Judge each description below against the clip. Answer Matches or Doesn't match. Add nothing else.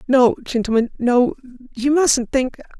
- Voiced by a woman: Matches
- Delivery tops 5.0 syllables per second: Doesn't match